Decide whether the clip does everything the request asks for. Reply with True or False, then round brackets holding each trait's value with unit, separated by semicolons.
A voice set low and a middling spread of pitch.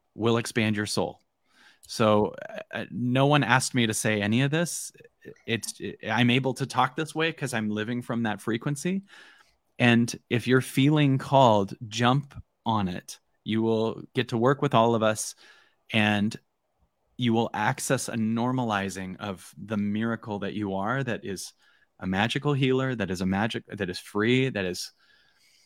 True (115 Hz; 3.6 semitones)